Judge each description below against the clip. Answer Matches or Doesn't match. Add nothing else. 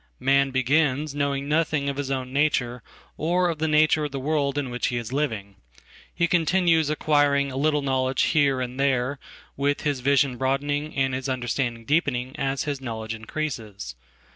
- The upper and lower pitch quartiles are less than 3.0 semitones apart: Matches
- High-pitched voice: Doesn't match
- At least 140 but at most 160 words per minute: Matches